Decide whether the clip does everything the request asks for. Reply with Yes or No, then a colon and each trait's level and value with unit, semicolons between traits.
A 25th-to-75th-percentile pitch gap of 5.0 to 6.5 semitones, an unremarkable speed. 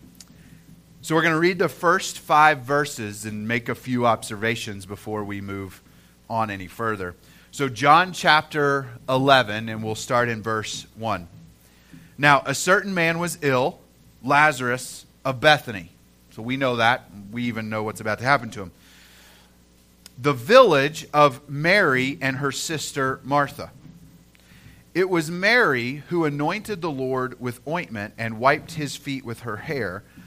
Yes: wide, 5.6 semitones; average, 150 wpm